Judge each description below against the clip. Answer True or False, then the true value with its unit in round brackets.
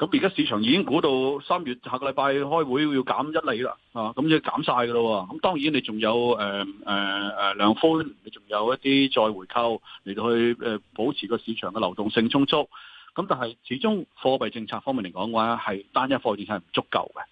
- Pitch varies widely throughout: False (4.0 semitones)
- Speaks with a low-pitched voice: True (120 Hz)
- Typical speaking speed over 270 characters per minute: True (310 characters per minute)